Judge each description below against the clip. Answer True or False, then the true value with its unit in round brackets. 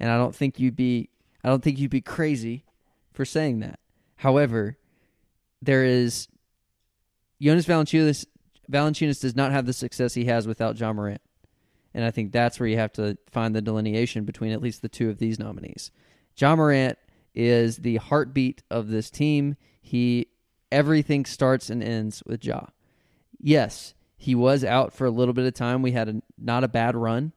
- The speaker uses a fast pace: False (180 wpm)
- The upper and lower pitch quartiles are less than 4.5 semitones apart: True (3.3 semitones)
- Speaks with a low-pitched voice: True (120 Hz)